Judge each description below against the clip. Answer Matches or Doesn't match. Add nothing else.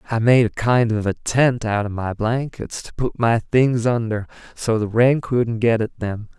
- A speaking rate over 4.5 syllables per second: Doesn't match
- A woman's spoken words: Doesn't match